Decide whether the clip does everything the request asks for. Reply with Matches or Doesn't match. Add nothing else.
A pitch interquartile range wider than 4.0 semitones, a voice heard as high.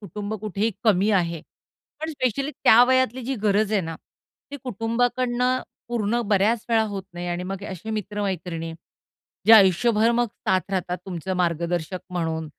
Matches